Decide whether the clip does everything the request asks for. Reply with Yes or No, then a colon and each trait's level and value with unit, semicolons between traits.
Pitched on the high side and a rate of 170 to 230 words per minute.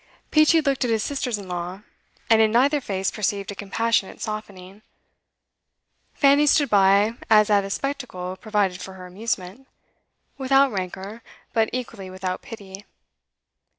No: high, 210 Hz; average, 140 wpm